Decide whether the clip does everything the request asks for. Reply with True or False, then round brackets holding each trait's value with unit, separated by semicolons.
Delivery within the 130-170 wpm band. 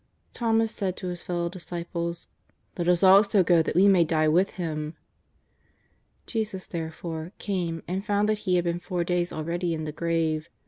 False (180 wpm)